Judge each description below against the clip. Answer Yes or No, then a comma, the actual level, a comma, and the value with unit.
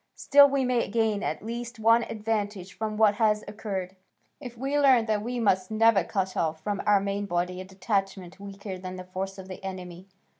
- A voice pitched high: Yes, high, 205 Hz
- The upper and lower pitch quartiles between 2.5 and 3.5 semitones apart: Yes, average, 3.1 semitones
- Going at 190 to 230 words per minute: Yes, average, 195 wpm